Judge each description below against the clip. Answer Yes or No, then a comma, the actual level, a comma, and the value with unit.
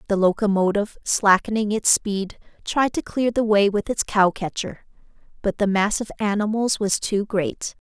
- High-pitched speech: Yes, high, 205 Hz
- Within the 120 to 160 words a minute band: No, average, 170 wpm